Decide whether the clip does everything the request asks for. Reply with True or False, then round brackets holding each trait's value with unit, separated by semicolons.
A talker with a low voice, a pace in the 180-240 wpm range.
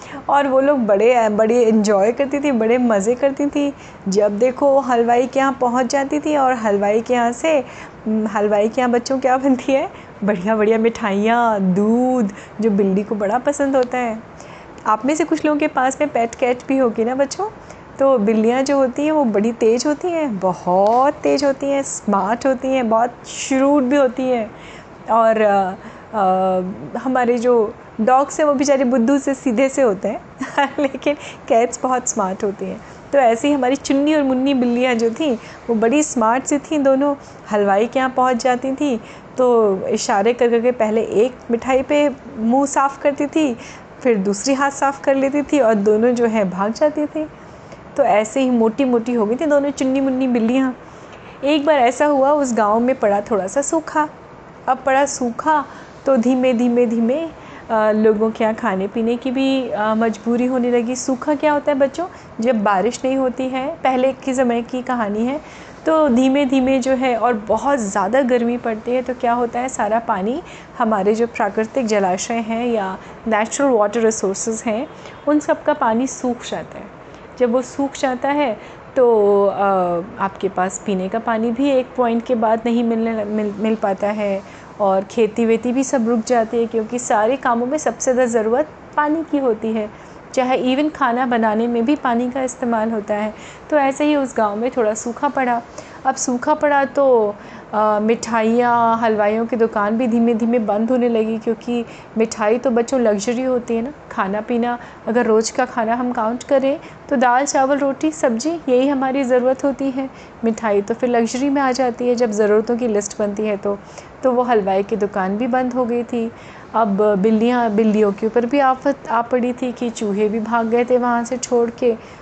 False (245 Hz; 190 wpm)